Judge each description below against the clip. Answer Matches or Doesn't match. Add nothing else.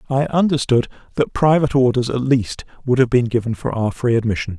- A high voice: Doesn't match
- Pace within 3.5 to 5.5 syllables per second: Doesn't match